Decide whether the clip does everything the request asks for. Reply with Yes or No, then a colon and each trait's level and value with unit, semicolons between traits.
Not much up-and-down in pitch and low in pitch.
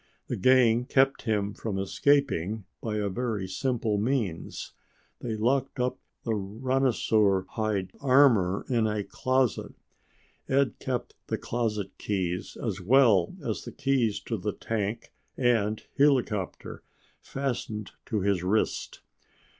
No: average, 4.2 semitones; low, 110 Hz